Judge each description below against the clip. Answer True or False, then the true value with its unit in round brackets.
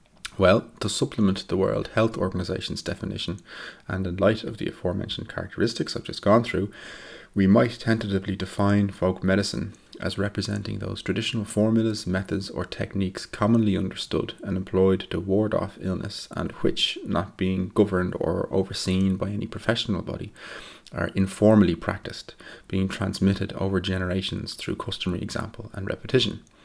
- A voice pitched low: True (100 Hz)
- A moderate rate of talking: True (145 wpm)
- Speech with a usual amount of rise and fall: False (2.0 semitones)